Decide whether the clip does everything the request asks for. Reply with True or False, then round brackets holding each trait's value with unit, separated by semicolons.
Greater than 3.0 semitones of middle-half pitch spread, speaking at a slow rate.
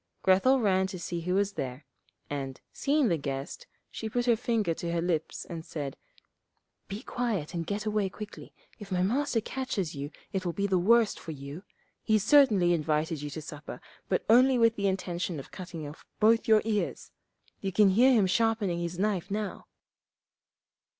False (4.8 semitones; 180 wpm)